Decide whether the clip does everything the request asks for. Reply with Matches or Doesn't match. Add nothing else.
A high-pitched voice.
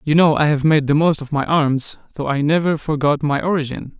Doesn't match